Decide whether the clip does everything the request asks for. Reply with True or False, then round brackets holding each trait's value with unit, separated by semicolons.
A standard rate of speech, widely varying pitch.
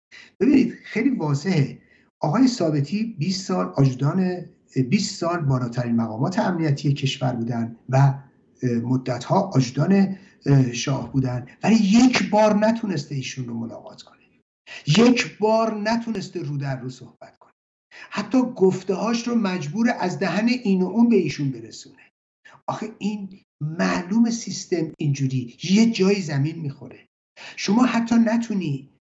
False (130 wpm; 7.9 semitones)